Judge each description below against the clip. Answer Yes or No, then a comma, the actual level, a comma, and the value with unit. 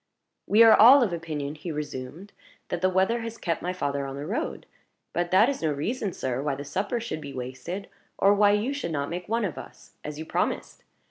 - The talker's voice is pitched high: No, medium, 175 Hz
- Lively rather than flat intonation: Yes, wide, 6.2 semitones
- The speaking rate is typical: No, fast, 220 wpm